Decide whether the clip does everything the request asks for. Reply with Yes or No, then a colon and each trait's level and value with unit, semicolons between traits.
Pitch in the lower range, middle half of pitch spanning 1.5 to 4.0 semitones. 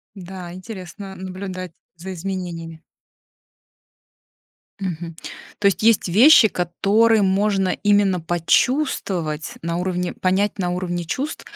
No: medium, 185 Hz; narrow, 2.4 semitones